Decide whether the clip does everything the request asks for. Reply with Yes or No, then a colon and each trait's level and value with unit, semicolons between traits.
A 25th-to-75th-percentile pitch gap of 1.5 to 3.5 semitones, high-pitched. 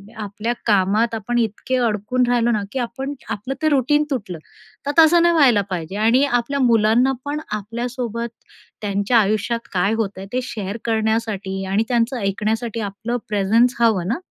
Yes: average, 3.1 semitones; high, 230 Hz